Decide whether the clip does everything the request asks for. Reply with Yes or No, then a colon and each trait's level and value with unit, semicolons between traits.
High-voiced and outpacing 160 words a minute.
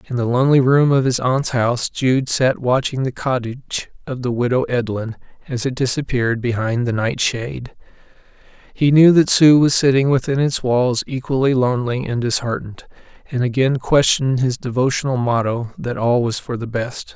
No: low, 125 Hz; average, 170 wpm